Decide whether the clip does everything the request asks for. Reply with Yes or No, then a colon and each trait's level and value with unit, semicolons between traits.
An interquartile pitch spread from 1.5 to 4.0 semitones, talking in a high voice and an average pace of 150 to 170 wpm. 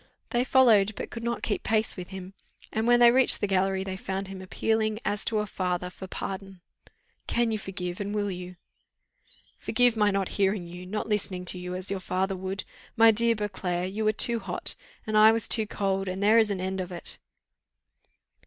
No: average, 2.7 semitones; high, 195 Hz; fast, 205 wpm